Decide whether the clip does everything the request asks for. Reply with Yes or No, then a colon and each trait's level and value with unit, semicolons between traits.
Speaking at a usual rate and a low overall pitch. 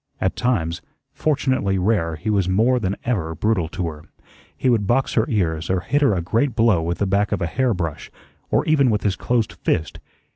No: fast, 210 wpm; low, 100 Hz